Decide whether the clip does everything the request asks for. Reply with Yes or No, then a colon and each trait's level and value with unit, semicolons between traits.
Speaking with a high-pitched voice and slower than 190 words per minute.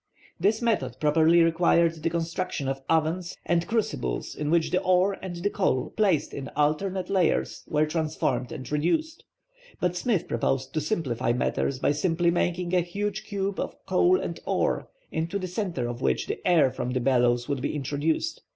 No: medium, 165 Hz; average, 175 wpm